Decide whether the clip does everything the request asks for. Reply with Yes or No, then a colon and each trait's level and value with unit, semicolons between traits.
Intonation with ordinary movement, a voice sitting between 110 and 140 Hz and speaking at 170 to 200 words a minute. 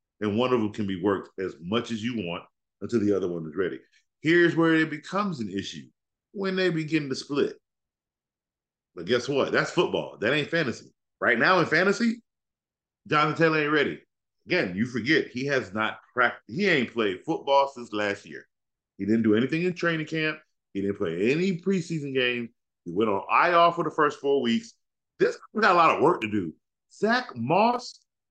No: wide, 8.0 semitones; low, 135 Hz; average, 195 wpm